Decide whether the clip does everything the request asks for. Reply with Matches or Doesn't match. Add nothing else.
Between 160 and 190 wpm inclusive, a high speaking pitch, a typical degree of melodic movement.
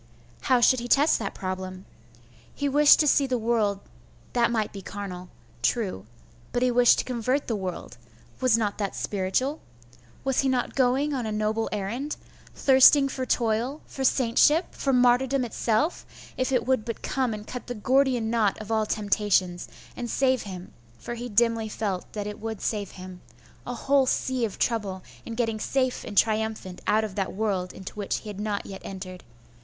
Matches